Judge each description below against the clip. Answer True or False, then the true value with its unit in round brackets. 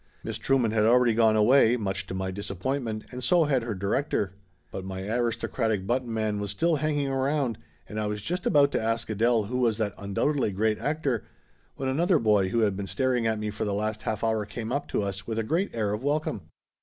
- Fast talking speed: True (230 wpm)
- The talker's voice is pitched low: True (110 Hz)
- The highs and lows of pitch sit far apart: False (4.0 semitones)